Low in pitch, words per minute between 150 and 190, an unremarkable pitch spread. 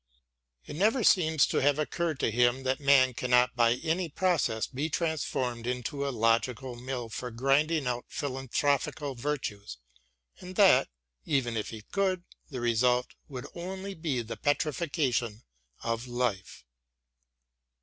No: low, 130 Hz; slow, 135 wpm; average, 4.3 semitones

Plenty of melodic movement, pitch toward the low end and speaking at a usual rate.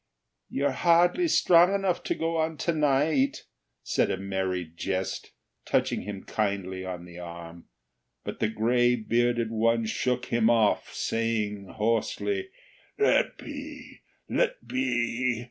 No: wide, 7.7 semitones; low, 115 Hz; slow, 130 wpm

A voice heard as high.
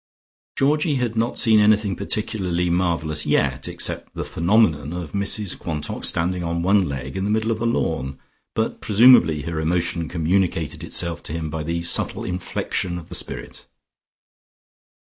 No: very low, 90 Hz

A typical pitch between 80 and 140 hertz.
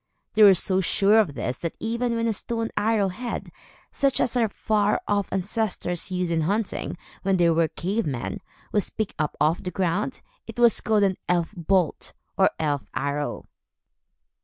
No: high, 195 Hz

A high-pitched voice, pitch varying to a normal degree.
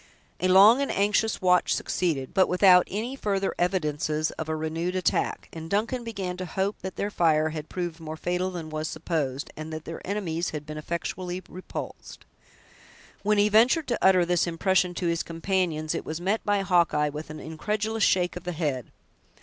No: medium, 180 Hz; average, 3.6 semitones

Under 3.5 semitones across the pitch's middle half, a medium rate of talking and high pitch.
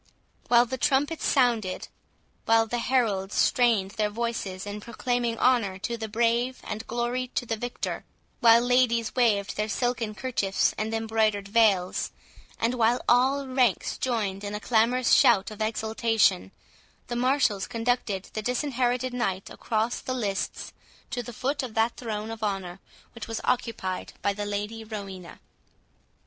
Yes: average, 2.8 semitones; average, 145 wpm; high, 225 Hz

